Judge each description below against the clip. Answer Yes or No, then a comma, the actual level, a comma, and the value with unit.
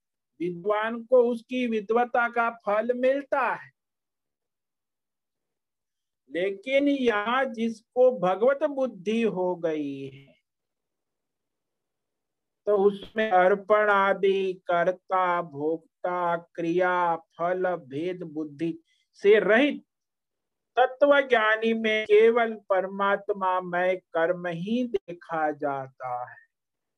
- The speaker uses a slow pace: Yes, slow, 85 wpm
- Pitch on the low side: No, high, 200 Hz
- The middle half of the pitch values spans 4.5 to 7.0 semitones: Yes, average, 5.2 semitones